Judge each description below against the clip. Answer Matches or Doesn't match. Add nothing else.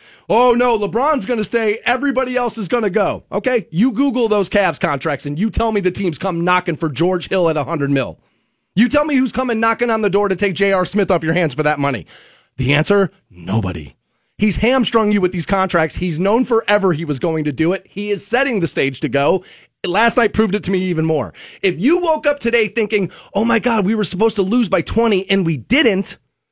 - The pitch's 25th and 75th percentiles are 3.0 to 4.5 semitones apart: Doesn't match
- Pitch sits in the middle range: Doesn't match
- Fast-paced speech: Matches